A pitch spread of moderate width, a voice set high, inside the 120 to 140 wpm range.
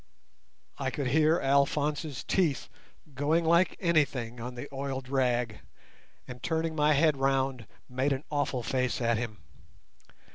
No: average, 3.2 semitones; low, 135 Hz; slow, 135 wpm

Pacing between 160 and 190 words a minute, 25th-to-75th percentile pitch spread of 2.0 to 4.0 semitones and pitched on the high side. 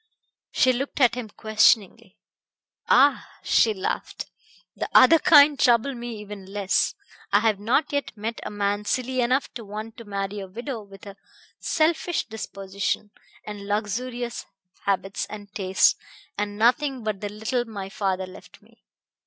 No: average, 150 wpm; average, 3.6 semitones; high, 215 Hz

